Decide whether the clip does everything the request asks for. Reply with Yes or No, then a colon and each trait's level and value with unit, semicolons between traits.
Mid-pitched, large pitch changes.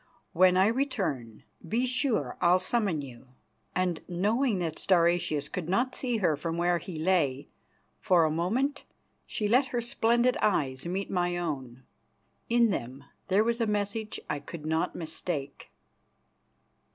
Yes: medium, 180 Hz; wide, 6.1 semitones